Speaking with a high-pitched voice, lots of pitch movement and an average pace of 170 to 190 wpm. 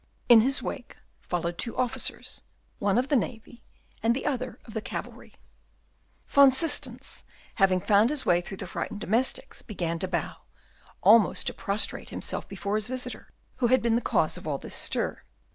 No: high, 230 Hz; average, 4.1 semitones; average, 175 wpm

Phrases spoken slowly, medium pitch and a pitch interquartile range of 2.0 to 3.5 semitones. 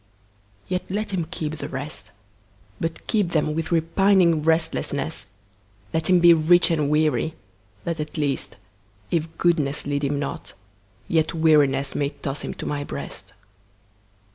Yes: slow, 125 wpm; medium, 155 Hz; average, 2.8 semitones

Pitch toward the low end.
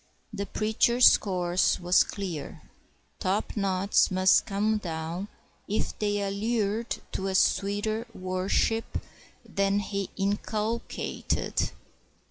No: high, 200 Hz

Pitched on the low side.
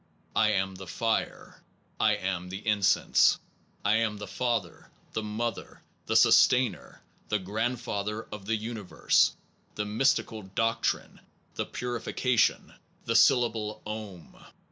Yes: low, 110 Hz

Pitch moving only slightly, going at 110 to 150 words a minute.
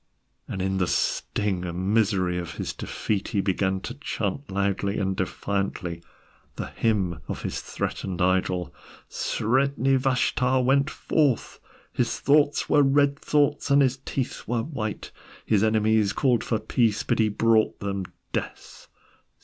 No: wide, 5.6 semitones; average, 140 wpm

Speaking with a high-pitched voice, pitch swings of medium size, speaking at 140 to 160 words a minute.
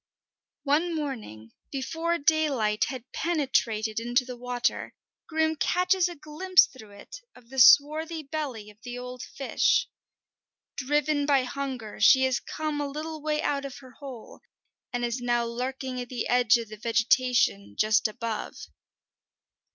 Yes: very high, 260 Hz; average, 4.1 semitones; average, 145 wpm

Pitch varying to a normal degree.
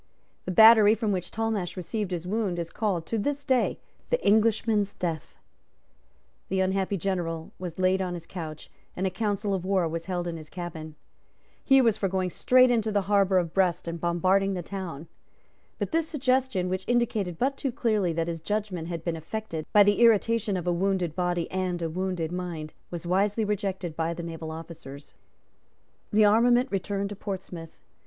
Yes: average, 3.7 semitones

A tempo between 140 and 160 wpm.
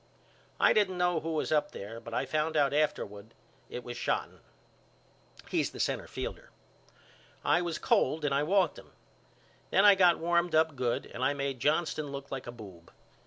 No: average, 175 wpm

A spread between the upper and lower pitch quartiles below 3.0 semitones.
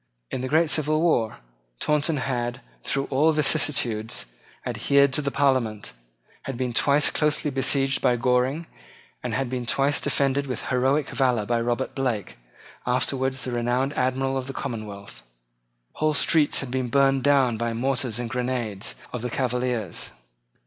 Yes: narrow, 2.4 semitones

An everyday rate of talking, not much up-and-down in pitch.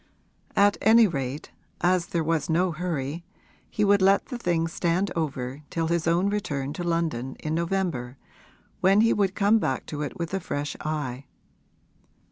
No: average, 165 wpm; average, 4.6 semitones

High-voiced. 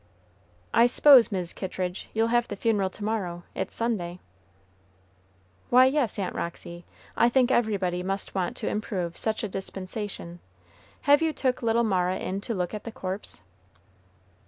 Yes: high, 205 Hz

